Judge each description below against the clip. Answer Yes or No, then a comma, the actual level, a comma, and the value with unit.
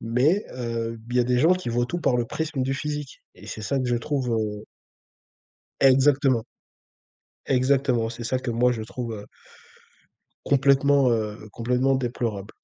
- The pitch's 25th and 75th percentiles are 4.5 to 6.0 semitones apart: No, average, 2.8 semitones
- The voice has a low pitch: Yes, low, 125 Hz